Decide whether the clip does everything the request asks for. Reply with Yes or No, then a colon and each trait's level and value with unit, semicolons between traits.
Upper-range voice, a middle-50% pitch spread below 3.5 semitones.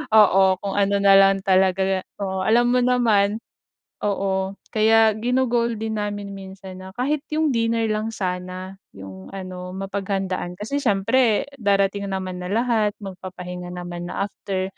Yes: high, 195 Hz; average, 2.8 semitones